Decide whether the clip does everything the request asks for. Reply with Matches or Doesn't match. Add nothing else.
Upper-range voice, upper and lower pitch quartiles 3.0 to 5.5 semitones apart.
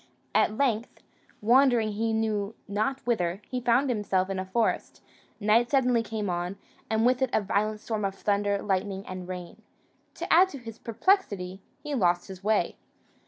Matches